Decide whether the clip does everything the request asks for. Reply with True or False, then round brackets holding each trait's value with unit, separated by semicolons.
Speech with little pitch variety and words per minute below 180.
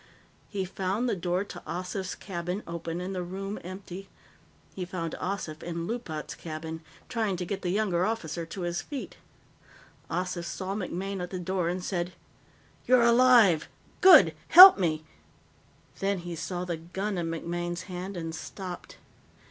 True (2.3 semitones; 155 wpm)